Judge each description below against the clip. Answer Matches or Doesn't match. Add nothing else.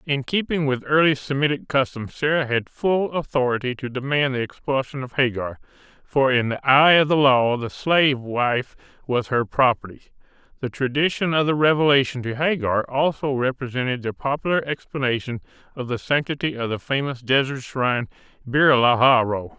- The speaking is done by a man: Matches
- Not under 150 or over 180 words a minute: Matches